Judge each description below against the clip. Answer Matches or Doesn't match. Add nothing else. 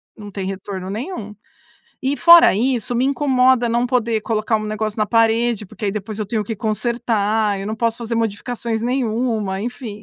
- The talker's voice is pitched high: Matches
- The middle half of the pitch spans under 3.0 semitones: Matches